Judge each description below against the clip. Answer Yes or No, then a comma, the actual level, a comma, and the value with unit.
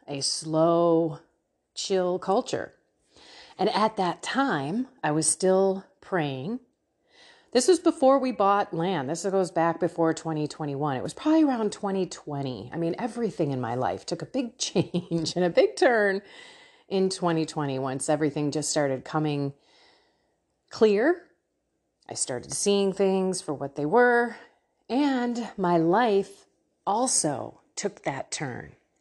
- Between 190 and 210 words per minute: No, slow, 135 wpm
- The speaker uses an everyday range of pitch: No, wide, 6.1 semitones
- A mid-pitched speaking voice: Yes, medium, 180 Hz